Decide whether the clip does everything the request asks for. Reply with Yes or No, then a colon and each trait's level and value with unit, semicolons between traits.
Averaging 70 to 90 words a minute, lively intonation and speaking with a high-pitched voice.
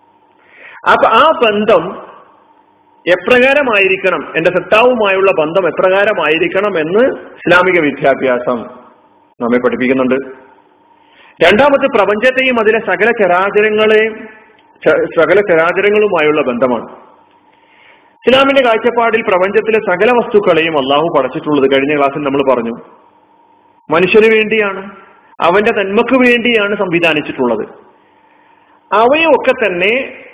Yes: average, 80 wpm; wide, 6.5 semitones; high, 210 Hz